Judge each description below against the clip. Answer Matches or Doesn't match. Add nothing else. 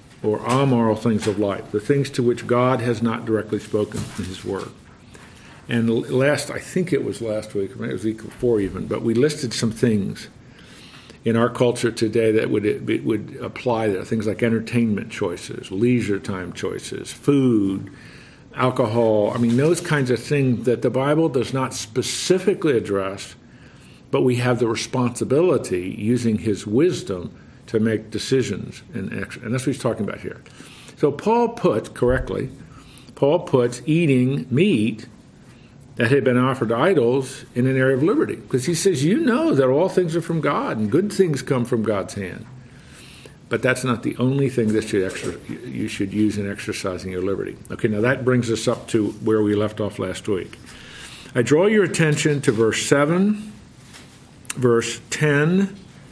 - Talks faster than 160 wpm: Matches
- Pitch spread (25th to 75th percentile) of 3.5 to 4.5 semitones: Matches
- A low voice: Matches